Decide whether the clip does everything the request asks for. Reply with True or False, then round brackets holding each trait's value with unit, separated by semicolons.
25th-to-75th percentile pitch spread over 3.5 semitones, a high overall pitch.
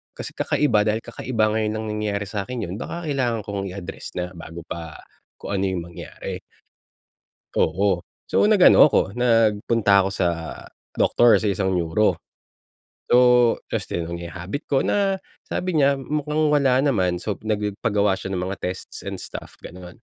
False (4.7 semitones; 105 Hz)